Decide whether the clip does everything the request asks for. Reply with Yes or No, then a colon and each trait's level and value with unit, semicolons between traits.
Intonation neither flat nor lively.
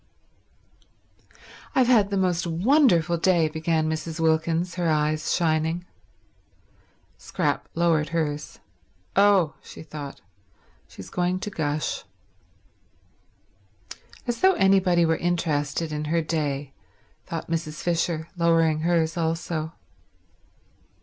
No: narrow, 2.0 semitones